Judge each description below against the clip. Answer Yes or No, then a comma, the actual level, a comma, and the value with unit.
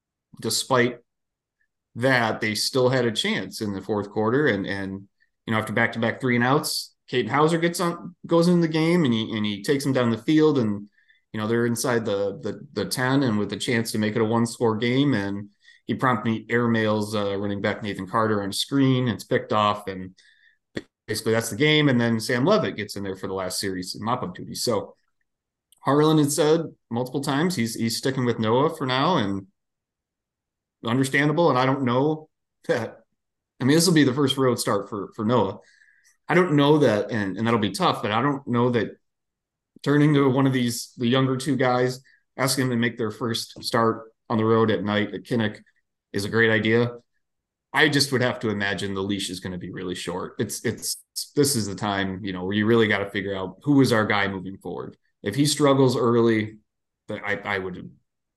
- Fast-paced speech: Yes, fast, 215 wpm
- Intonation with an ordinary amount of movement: Yes, average, 4.4 semitones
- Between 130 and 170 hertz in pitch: No, low, 115 Hz